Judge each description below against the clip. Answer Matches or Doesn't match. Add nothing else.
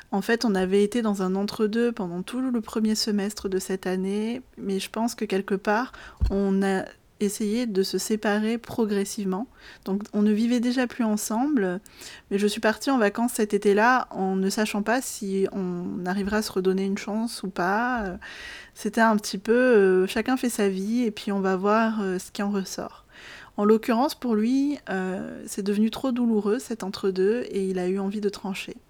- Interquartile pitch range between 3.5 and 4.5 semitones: Doesn't match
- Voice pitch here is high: Matches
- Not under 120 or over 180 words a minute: Doesn't match